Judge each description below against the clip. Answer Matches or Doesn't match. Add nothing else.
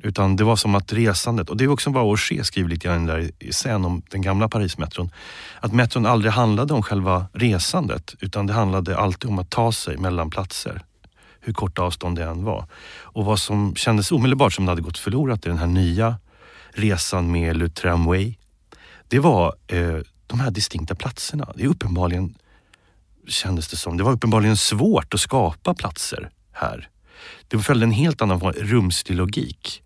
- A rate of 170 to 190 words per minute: Matches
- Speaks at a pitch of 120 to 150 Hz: Doesn't match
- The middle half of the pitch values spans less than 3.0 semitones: Doesn't match